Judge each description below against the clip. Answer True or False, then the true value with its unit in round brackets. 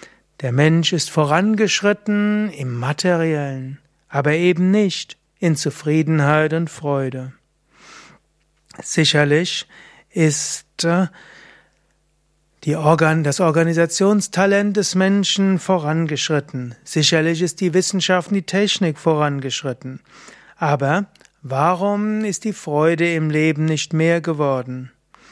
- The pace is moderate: False (95 wpm)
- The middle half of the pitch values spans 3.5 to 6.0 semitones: True (3.9 semitones)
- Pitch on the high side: False (160 Hz)